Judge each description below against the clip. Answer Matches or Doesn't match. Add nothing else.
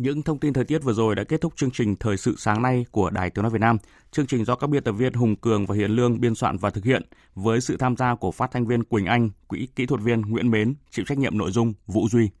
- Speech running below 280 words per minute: Doesn't match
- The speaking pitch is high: Doesn't match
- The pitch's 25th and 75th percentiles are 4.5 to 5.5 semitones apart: Doesn't match